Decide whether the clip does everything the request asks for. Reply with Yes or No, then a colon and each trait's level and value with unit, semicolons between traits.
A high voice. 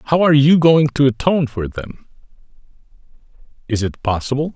No: low, 135 Hz